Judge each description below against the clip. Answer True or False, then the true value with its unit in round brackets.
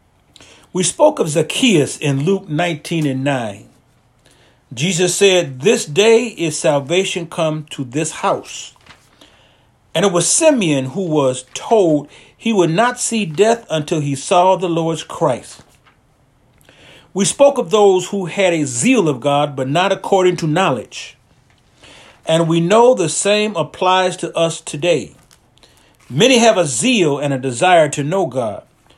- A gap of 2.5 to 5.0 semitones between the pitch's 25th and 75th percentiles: False (5.4 semitones)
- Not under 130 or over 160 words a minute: True (145 wpm)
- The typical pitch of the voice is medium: True (165 Hz)